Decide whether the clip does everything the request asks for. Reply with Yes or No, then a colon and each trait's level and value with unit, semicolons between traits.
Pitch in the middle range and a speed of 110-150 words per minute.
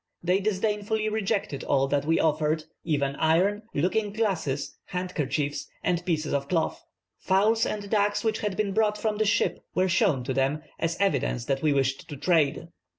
No: medium, 175 Hz; average, 170 wpm